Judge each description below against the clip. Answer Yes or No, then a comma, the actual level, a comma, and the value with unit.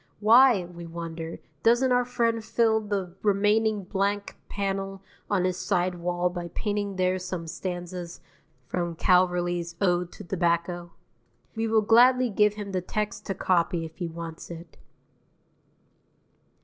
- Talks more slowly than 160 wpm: Yes, slow, 135 wpm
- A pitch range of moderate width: Yes, average, 3.3 semitones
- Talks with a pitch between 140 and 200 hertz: Yes, medium, 185 Hz